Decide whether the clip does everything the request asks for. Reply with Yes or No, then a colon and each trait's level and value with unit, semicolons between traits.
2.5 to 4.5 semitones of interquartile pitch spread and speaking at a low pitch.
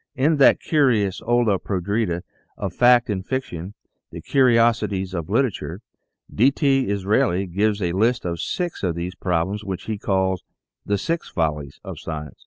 No: average, 5.0 semitones; low, 100 Hz